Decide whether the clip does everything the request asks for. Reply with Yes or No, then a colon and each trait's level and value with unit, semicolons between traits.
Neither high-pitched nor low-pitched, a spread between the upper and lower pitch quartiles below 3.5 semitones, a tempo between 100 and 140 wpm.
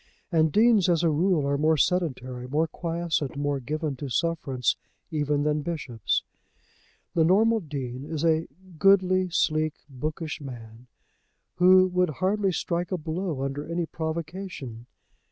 No: medium, 160 Hz; average, 3.8 semitones; slow, 135 wpm